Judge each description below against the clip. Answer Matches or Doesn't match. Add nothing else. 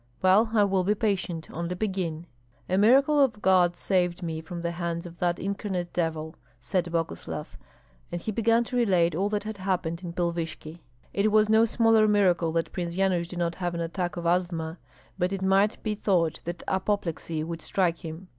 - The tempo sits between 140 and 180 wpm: Doesn't match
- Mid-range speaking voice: Matches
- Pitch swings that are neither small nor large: Matches